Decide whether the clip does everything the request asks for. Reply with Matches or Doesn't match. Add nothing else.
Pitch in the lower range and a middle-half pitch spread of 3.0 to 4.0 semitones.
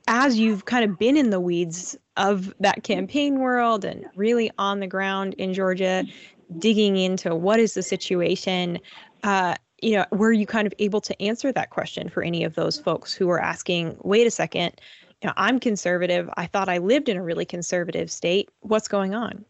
Doesn't match